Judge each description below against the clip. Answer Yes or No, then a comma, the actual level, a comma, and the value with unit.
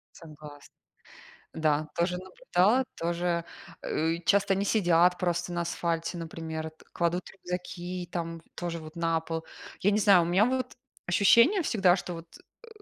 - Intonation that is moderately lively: No, narrow, 2.1 semitones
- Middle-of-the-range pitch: Yes, medium, 175 Hz